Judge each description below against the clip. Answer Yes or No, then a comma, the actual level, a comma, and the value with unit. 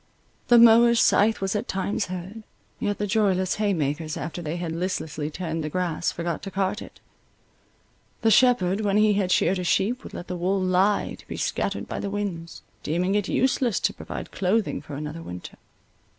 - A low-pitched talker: No, high, 190 Hz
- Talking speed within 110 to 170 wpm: No, average, 185 wpm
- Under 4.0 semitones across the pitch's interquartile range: Yes, average, 3.6 semitones